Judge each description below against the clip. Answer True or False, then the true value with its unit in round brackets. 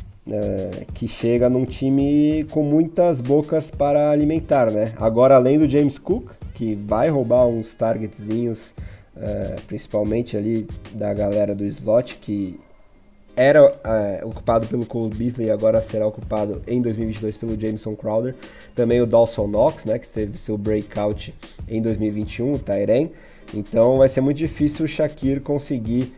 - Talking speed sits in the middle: True (150 wpm)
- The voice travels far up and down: False (4.1 semitones)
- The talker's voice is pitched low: True (115 Hz)